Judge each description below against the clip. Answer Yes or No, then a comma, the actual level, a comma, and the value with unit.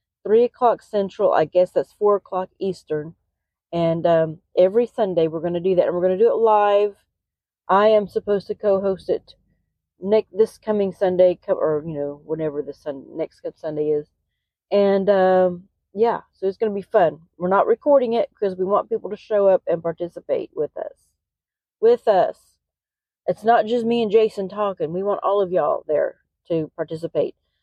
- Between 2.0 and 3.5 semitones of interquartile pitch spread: No, average, 4.2 semitones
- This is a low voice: No, high, 195 Hz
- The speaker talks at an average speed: Yes, average, 185 wpm